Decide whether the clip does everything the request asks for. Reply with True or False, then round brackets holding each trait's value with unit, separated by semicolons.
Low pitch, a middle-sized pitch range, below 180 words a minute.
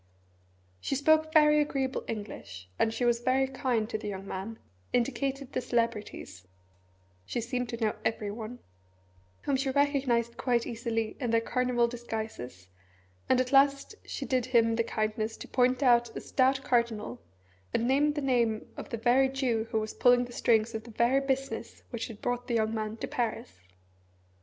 False (240 Hz; 3.0 semitones; 170 wpm)